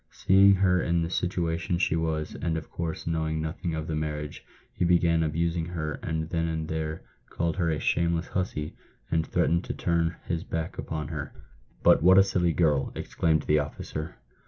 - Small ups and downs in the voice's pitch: Yes, narrow, 1.6 semitones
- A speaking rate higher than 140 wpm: Yes, average, 185 wpm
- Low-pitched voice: Yes, very low, 80 Hz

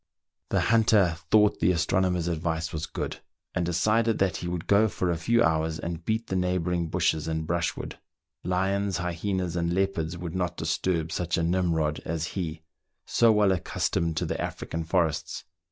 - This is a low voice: Yes, very low, 85 Hz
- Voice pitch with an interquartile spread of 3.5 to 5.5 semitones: No, narrow, 2.5 semitones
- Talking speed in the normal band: Yes, average, 170 wpm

